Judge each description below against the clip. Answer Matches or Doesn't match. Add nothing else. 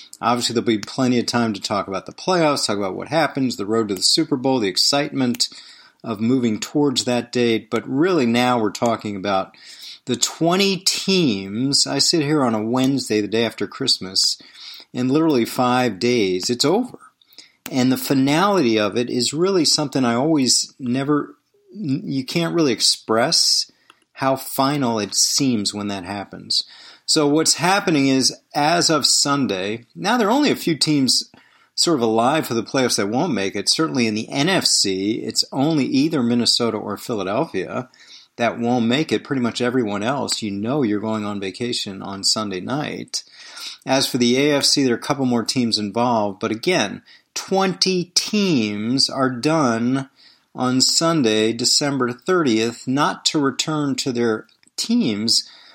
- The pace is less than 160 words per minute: Doesn't match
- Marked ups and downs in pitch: Doesn't match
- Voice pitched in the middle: Doesn't match